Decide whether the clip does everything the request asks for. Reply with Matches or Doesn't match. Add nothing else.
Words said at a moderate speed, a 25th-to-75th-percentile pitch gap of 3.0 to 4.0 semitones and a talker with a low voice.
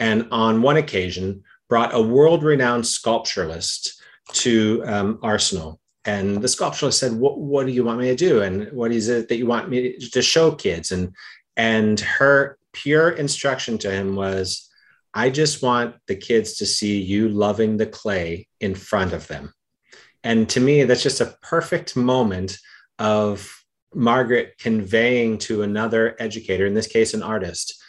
Matches